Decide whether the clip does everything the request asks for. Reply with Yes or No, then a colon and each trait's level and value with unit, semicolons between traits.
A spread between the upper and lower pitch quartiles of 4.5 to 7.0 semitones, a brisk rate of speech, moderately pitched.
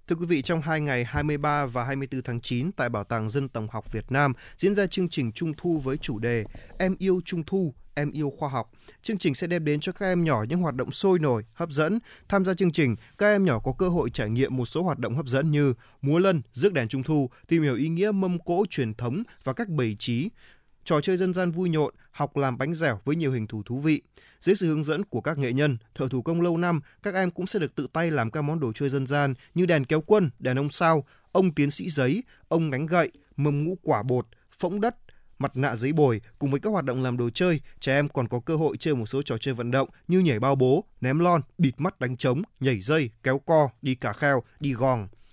Yes: average, 5.0 semitones; fast, 260 wpm; medium, 145 Hz